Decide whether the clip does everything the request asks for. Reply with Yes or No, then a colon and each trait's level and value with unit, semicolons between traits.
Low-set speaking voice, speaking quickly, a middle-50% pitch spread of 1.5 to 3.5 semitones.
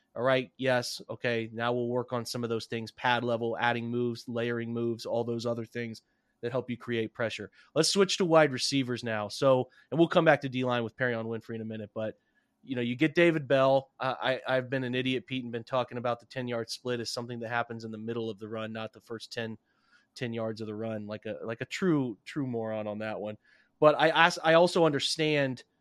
Yes: low, 120 Hz; fast, 240 wpm; narrow, 2.5 semitones